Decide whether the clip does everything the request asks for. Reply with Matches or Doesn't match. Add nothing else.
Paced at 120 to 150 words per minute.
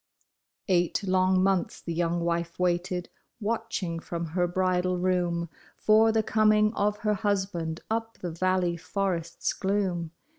Matches